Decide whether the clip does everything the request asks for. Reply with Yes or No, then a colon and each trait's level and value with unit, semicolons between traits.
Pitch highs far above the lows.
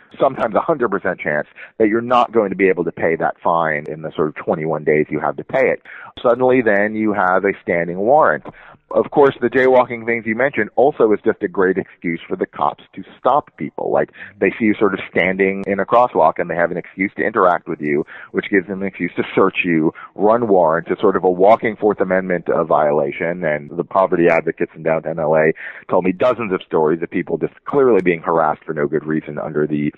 No: average, 4.8 semitones